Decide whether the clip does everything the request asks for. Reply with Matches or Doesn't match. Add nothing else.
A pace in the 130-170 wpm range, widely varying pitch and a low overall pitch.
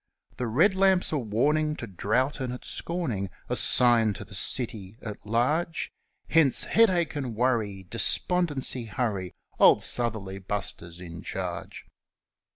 Matches